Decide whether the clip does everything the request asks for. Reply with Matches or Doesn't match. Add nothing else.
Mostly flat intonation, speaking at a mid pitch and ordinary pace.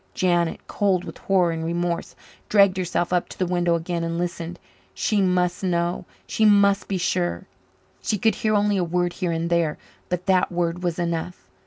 Matches